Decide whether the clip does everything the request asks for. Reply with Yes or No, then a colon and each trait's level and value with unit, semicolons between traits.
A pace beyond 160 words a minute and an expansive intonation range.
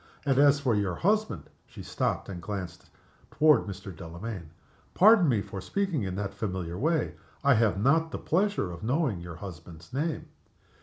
Yes: average, 170 wpm; wide, 8.9 semitones